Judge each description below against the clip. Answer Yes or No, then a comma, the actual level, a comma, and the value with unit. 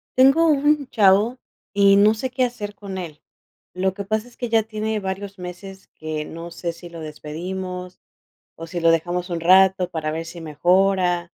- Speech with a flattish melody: No, average, 3.7 semitones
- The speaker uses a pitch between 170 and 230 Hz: Yes, high, 190 Hz